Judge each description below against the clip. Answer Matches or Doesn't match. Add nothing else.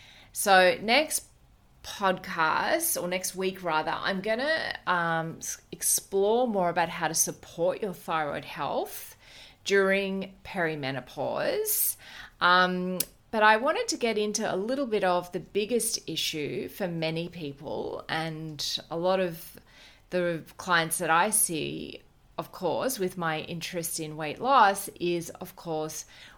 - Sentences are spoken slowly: Matches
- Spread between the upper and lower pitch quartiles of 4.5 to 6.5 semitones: Doesn't match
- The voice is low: Doesn't match